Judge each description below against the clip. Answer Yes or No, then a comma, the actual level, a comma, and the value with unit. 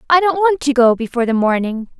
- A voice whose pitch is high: Yes, very high, 270 Hz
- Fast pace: Yes, fast, 240 wpm